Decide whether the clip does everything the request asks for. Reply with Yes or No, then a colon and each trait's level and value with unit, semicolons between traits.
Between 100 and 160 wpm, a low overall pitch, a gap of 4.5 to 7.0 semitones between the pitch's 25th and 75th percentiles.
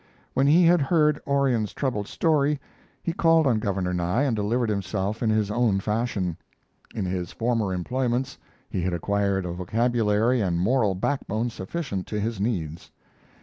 Yes: average, 155 wpm; low, 110 Hz; average, 5.2 semitones